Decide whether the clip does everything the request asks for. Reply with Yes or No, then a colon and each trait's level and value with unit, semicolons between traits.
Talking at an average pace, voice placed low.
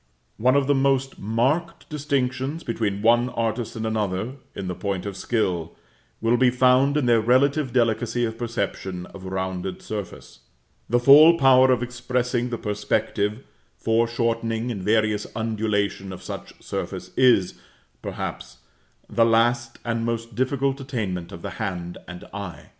Yes: average, 145 wpm; low, 115 Hz